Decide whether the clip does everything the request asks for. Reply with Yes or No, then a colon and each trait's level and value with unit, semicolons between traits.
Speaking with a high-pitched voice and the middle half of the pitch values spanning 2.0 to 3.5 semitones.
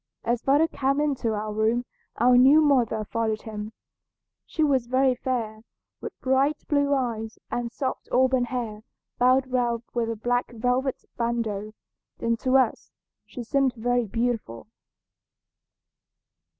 Yes: high, 245 Hz; narrow, 2.6 semitones